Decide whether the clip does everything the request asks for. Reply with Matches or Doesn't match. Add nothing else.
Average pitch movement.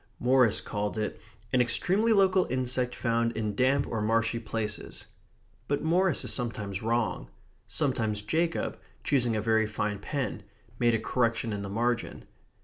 Matches